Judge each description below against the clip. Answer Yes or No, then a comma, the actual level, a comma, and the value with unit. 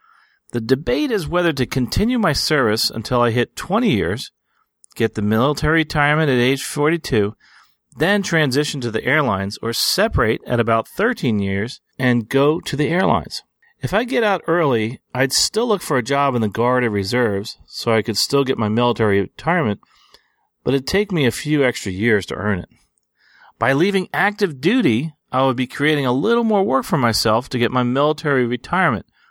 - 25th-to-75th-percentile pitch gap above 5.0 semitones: Yes, wide, 5.5 semitones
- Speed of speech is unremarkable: Yes, average, 185 wpm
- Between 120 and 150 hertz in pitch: Yes, low, 135 Hz